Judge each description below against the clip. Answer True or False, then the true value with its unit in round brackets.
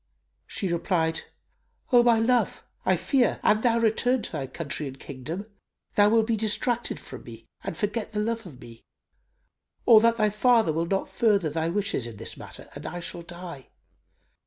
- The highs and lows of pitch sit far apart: True (5.8 semitones)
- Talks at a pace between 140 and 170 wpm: False (180 wpm)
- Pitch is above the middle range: True (205 Hz)